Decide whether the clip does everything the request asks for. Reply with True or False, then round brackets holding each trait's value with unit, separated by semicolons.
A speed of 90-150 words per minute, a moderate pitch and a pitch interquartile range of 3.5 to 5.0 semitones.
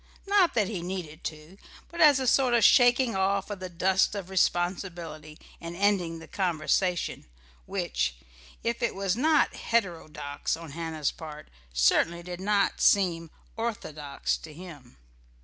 True (145 wpm; 180 Hz; 4.1 semitones)